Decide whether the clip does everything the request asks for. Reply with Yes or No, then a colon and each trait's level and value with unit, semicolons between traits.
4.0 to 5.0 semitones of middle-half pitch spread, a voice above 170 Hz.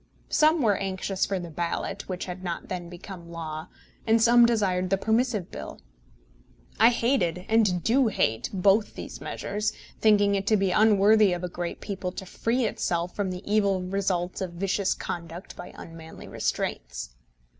No: average, 3.3 semitones; high, 190 Hz